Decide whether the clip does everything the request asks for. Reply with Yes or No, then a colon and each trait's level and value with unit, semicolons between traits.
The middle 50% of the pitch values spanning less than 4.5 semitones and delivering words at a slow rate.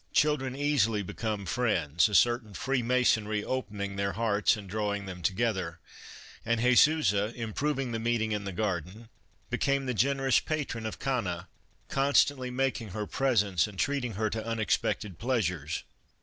No: average, 4.1 semitones; average, 150 wpm